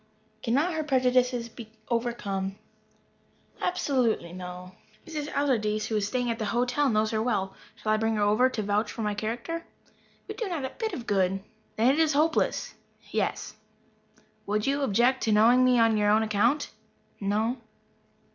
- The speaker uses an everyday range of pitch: Yes, average, 3.7 semitones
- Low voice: No, high, 230 Hz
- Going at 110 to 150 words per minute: No, average, 170 wpm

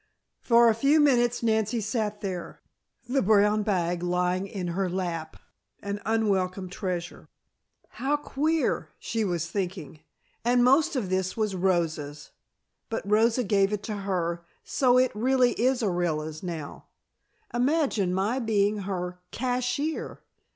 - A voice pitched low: No, high, 205 Hz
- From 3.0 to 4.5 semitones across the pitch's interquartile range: No, average, 5.0 semitones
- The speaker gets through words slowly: Yes, slow, 130 wpm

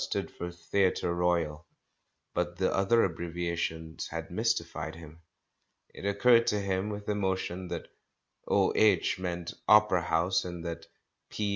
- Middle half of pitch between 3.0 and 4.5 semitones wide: No, narrow, 2.5 semitones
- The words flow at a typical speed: No, slow, 130 wpm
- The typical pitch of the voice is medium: No, very low, 90 Hz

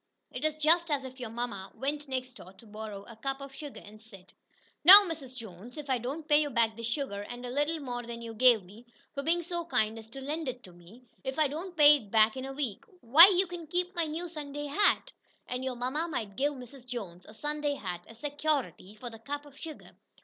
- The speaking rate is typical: No, fast, 240 wpm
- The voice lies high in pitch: Yes, very high, 265 Hz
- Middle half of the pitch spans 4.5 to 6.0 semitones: Yes, average, 4.9 semitones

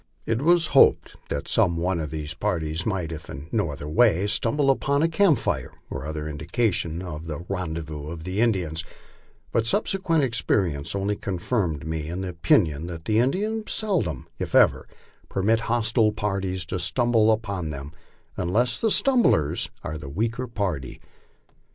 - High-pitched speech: No, very low, 95 Hz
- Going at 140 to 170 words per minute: Yes, average, 160 wpm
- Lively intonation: Yes, wide, 6.6 semitones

